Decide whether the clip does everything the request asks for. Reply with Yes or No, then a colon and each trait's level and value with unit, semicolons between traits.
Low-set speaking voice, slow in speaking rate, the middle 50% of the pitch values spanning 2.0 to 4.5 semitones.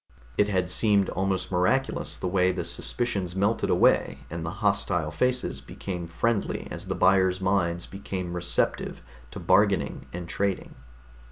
No: very low, 95 Hz; average, 145 wpm; narrow, 2.4 semitones